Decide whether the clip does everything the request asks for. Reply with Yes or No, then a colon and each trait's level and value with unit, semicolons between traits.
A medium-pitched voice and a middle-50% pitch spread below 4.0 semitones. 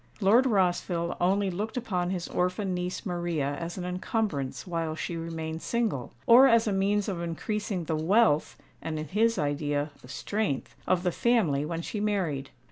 No: medium, 180 Hz; average, 4.4 semitones